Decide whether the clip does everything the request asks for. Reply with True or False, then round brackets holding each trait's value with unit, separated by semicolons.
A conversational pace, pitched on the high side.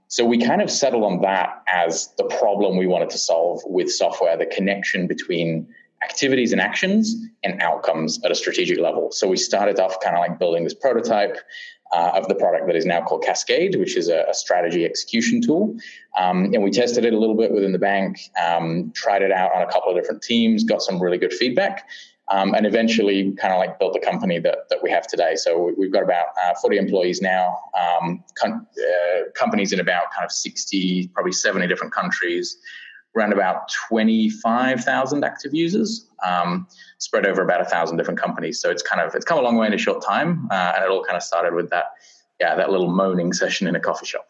False (220 wpm; 225 Hz)